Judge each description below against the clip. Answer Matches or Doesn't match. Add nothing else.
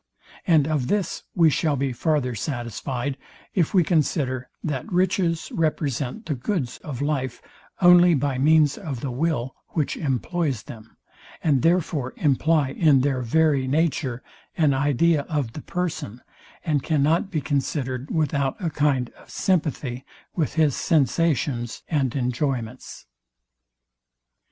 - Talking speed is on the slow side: Matches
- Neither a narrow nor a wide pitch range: Matches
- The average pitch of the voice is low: Doesn't match